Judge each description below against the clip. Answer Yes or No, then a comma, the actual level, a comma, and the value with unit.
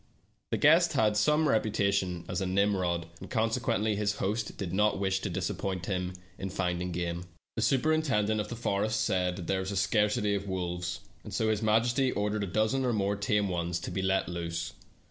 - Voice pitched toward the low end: Yes, low, 100 Hz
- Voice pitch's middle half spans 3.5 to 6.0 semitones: No, average, 2.9 semitones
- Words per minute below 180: No, average, 190 wpm